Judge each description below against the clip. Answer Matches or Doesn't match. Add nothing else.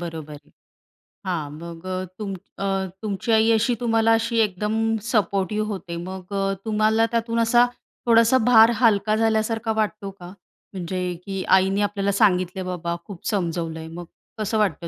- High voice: Matches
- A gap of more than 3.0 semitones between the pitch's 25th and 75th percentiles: Matches